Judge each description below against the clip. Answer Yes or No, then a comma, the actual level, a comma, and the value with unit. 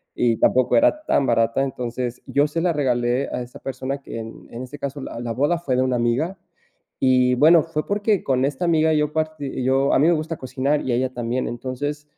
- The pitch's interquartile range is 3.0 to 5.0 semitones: Yes, average, 3.5 semitones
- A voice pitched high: No, low, 135 Hz